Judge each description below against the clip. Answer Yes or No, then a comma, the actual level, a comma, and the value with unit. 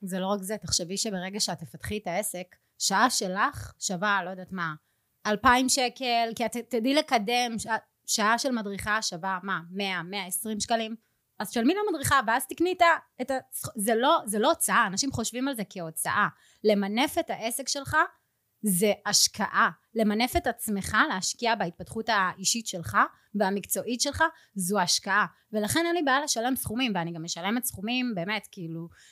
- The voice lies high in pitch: Yes, high, 220 Hz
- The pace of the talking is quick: Yes, fast, 160 wpm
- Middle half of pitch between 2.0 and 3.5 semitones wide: No, average, 4.7 semitones